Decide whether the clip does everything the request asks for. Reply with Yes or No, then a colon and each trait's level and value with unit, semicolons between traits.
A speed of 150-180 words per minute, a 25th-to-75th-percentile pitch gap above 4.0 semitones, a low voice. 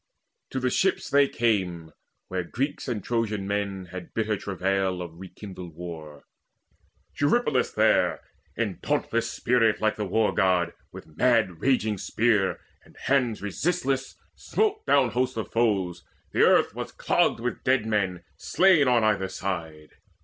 No: average, 140 wpm; average, 5.1 semitones; low, 105 Hz